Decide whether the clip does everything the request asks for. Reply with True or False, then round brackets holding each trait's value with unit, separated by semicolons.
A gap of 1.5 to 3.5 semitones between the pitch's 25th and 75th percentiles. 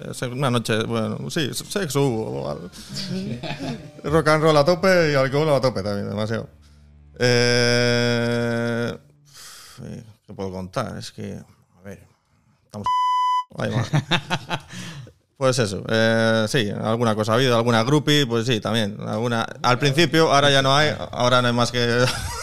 False (4.6 semitones)